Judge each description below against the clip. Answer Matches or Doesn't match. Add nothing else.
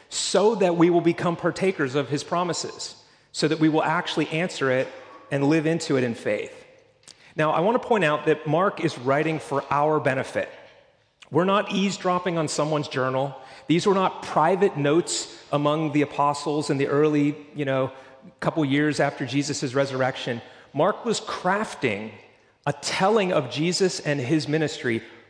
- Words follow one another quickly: Doesn't match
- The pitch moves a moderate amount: Matches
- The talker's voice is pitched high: Doesn't match